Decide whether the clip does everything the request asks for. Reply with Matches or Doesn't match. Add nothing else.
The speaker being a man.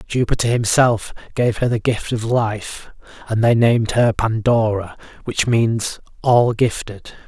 Matches